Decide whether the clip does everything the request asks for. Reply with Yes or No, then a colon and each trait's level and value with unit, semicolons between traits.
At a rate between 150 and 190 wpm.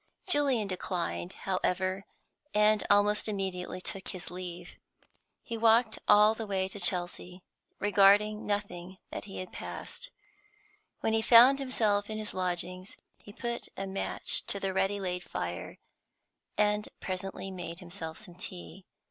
No: slow, 135 wpm